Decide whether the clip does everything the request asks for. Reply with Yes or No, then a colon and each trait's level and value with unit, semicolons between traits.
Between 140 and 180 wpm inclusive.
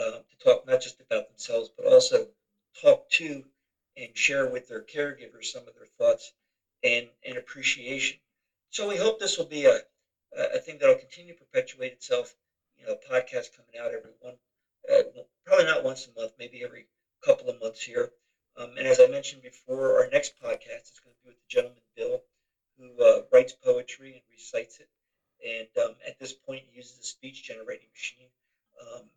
No: average, 195 wpm